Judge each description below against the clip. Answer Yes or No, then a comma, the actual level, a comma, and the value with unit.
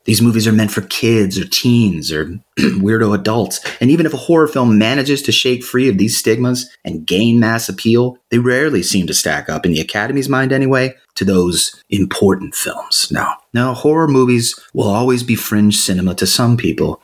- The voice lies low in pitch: Yes, low, 120 Hz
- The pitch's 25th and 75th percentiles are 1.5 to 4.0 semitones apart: Yes, average, 2.9 semitones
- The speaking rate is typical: Yes, average, 195 wpm